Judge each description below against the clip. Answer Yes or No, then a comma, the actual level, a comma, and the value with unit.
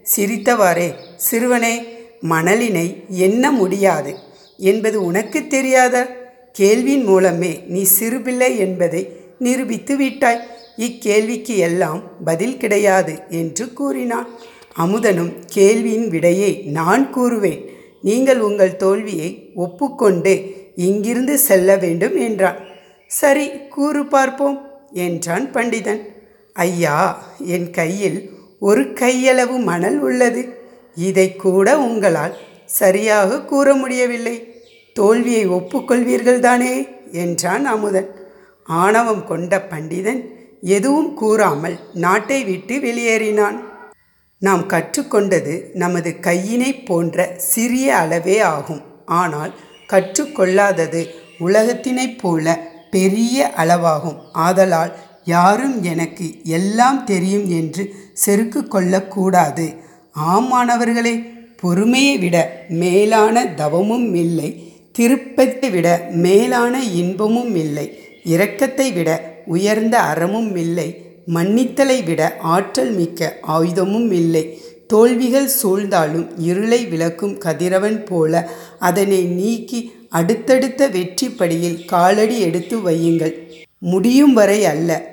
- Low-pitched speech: No, high, 195 Hz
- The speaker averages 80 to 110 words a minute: Yes, average, 90 wpm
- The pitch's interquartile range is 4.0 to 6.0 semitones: Yes, average, 5.3 semitones